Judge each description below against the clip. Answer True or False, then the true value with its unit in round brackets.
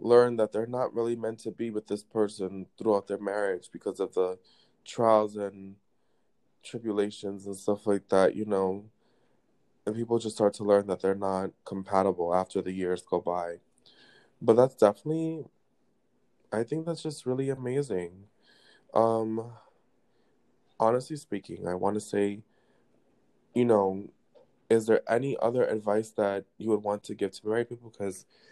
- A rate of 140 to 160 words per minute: True (155 wpm)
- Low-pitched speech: True (105 Hz)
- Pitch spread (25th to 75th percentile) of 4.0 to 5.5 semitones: False (2.8 semitones)